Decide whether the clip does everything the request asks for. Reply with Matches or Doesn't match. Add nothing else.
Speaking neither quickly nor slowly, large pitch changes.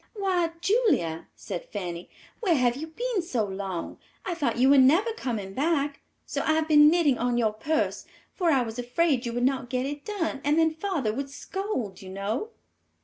Matches